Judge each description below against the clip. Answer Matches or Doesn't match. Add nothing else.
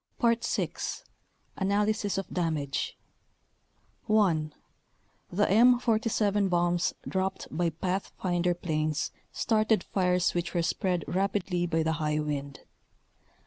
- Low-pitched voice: Doesn't match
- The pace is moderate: Doesn't match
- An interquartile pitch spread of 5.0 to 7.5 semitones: Doesn't match